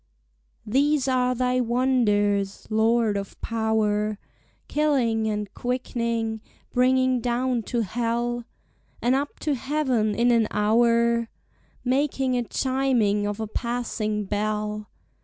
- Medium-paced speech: No, slow, 110 wpm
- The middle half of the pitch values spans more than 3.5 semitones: No, average, 2.9 semitones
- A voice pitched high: Yes, high, 235 Hz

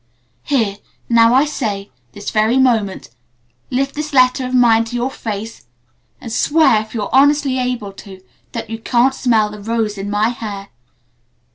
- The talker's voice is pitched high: Yes, high, 230 Hz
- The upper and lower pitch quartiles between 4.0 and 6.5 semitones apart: No, average, 3.4 semitones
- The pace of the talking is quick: No, average, 160 wpm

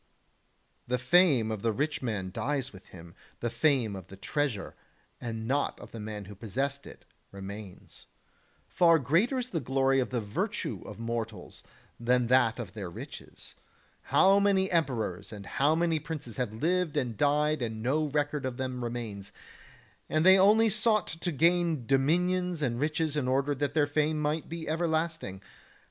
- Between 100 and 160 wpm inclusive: No, average, 170 wpm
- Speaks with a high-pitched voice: No, low, 135 Hz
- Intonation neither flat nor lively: No, wide, 6.0 semitones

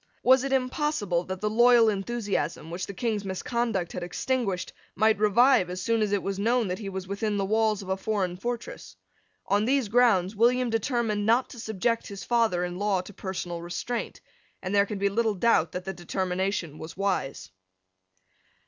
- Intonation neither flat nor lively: Yes, average, 3.8 semitones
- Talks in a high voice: Yes, high, 205 Hz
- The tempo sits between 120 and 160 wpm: No, average, 185 wpm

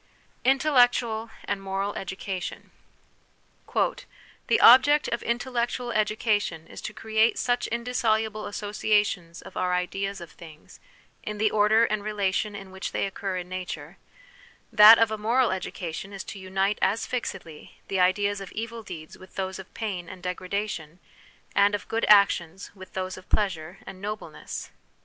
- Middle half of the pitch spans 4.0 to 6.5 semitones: No, average, 2.7 semitones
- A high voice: Yes, high, 200 Hz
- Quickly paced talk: No, average, 150 wpm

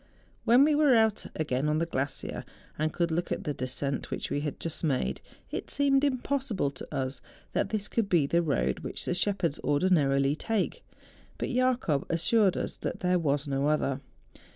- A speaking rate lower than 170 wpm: No, average, 185 wpm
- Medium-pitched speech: Yes, medium, 165 Hz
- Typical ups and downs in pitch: No, wide, 7.9 semitones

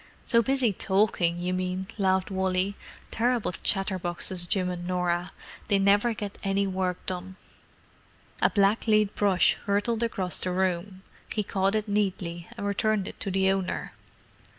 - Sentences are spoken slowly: No, average, 145 wpm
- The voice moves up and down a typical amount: No, narrow, 2.0 semitones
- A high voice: Yes, high, 195 Hz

